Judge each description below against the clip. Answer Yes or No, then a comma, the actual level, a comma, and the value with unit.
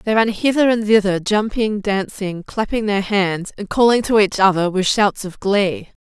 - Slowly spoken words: No, average, 190 wpm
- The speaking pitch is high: Yes, high, 205 Hz